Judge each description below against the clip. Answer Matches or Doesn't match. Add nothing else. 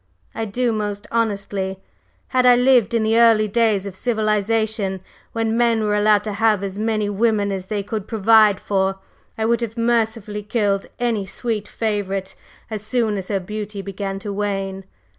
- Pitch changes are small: Matches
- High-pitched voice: Matches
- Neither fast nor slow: Matches